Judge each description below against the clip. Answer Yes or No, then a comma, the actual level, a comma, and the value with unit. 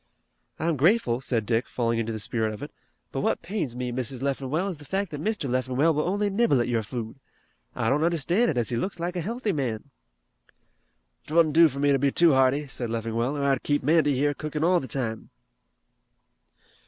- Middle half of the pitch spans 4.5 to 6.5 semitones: Yes, wide, 5.4 semitones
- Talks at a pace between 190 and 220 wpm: Yes, fast, 205 wpm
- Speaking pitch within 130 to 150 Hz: Yes, medium, 140 Hz